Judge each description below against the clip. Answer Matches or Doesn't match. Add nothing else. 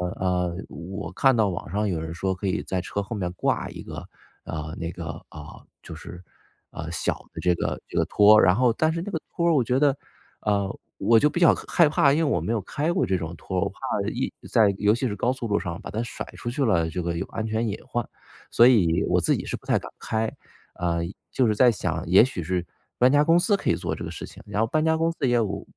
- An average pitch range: Doesn't match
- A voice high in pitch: Doesn't match